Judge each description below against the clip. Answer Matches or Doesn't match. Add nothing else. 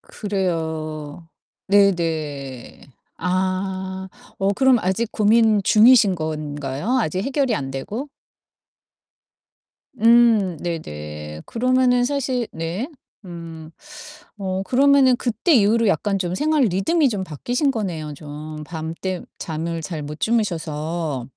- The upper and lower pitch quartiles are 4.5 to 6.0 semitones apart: Doesn't match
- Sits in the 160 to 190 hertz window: Matches